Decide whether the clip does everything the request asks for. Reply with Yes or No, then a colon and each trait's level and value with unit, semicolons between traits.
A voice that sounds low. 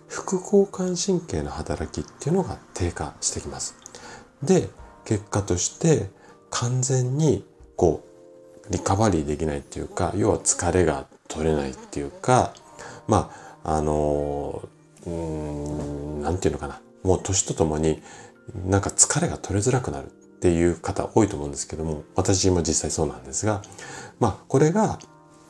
Yes: very low, 85 Hz